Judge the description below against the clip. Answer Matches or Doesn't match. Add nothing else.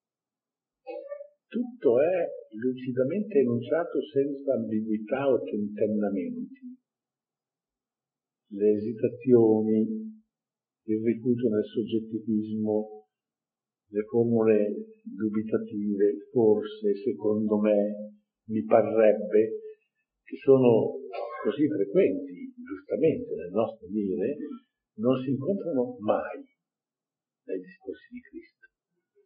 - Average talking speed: Doesn't match